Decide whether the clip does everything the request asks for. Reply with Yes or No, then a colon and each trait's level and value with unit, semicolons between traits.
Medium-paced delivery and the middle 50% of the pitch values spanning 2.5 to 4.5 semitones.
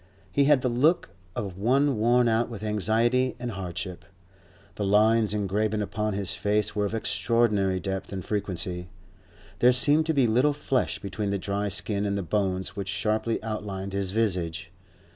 Yes: average, 165 wpm; average, 3.2 semitones